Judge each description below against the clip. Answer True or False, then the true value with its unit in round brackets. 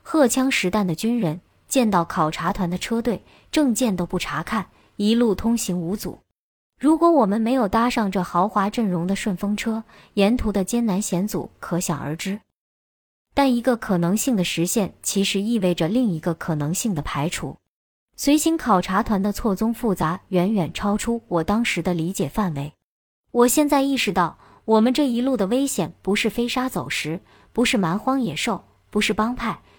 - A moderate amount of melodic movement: True (4.8 semitones)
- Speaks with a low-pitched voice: False (210 Hz)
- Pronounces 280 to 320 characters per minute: False (260 characters per minute)